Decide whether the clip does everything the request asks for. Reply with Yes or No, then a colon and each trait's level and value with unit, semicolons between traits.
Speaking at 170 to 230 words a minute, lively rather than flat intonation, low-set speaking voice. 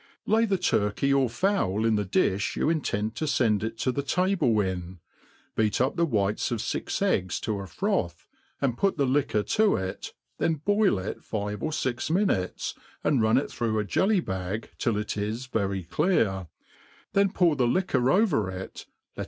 Yes: average, 180 wpm; wide, 7.5 semitones; low, 115 Hz